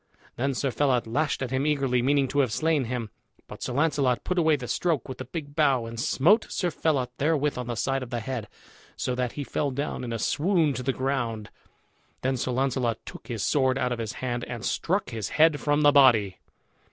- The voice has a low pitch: Yes, low, 130 Hz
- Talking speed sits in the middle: No, fast, 220 wpm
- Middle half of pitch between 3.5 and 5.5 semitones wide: No, average, 3.1 semitones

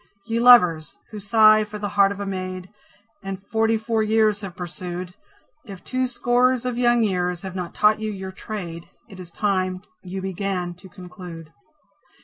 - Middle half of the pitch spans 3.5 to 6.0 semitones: No, average, 3.1 semitones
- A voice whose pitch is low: No, high, 195 Hz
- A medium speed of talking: Yes, average, 170 wpm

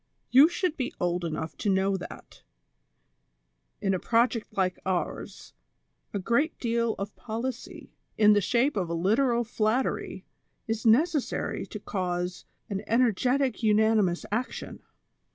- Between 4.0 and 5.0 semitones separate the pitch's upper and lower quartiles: Yes, average, 4.5 semitones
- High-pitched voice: Yes, high, 220 Hz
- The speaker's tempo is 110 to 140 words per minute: Yes, slow, 135 wpm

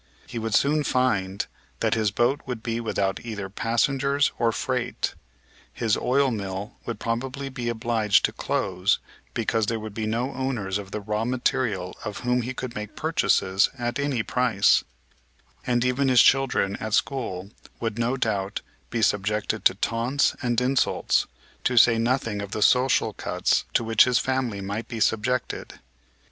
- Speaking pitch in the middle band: No, low, 115 Hz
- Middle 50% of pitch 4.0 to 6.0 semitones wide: No, average, 3.3 semitones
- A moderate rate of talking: Yes, average, 160 wpm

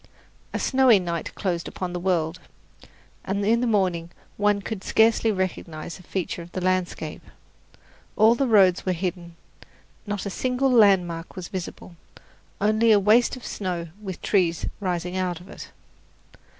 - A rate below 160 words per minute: Yes, average, 150 wpm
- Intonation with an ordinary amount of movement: Yes, average, 3.3 semitones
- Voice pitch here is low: No, high, 190 Hz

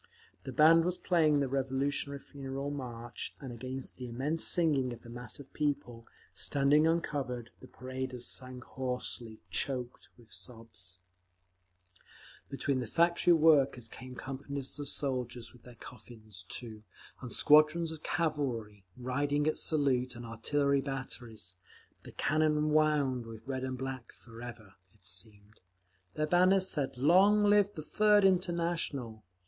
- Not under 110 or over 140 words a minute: Yes, slow, 135 wpm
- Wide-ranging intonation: No, average, 4.0 semitones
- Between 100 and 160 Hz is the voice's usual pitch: Yes, low, 135 Hz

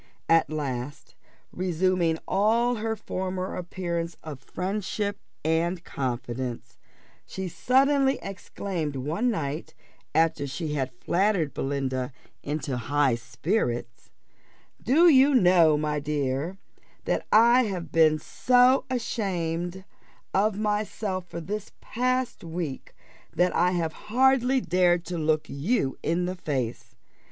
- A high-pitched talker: No, medium, 175 Hz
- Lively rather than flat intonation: Yes, wide, 6.0 semitones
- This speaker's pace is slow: Yes, slow, 115 wpm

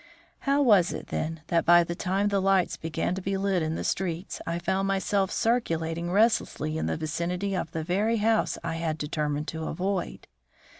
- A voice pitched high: No, medium, 180 Hz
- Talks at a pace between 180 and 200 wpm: Yes, average, 190 wpm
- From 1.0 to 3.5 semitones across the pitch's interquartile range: Yes, average, 3.2 semitones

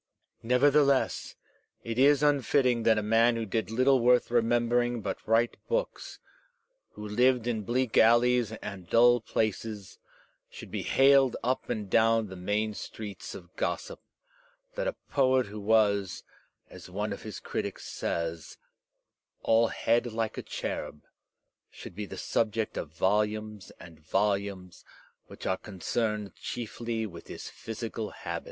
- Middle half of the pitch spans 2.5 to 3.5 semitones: Yes, average, 2.9 semitones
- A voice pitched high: No, low, 115 Hz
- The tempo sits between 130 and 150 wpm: Yes, average, 140 wpm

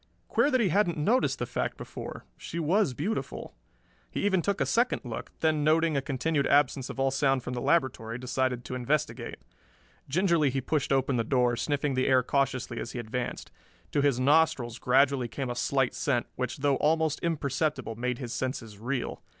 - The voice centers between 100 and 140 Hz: Yes, low, 135 Hz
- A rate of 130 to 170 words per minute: No, average, 185 wpm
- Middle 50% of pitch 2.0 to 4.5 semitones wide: Yes, average, 3.8 semitones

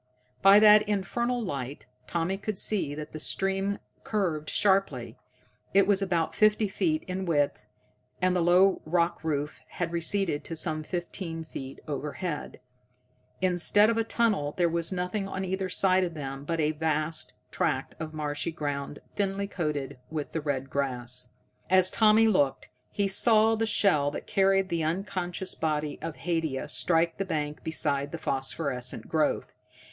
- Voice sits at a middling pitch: Yes, medium, 170 Hz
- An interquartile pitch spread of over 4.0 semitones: Yes, average, 4.4 semitones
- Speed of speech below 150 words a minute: No, average, 155 wpm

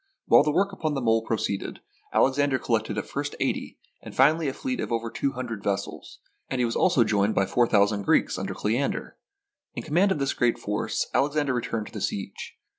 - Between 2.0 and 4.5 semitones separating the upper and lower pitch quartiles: No, average, 4.9 semitones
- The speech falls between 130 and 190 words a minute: No, fast, 205 wpm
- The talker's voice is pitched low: Yes, low, 120 Hz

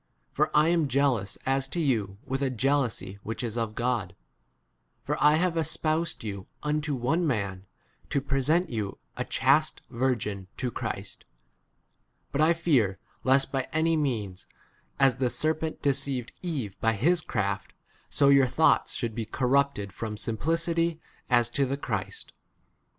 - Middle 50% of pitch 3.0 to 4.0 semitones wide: No, average, 5.3 semitones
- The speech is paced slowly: No, average, 160 wpm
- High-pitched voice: No, low, 130 Hz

